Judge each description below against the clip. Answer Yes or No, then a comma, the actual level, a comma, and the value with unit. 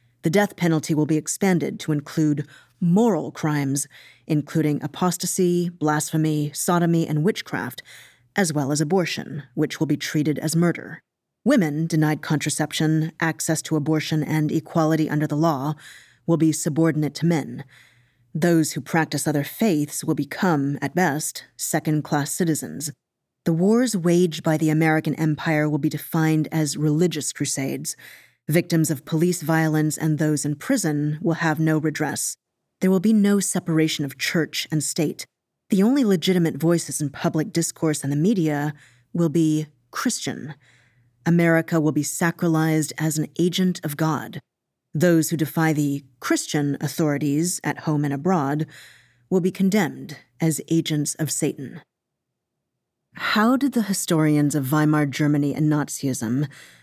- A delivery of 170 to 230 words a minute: No, average, 145 wpm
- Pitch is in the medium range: Yes, medium, 155 Hz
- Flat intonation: Yes, narrow, 2.1 semitones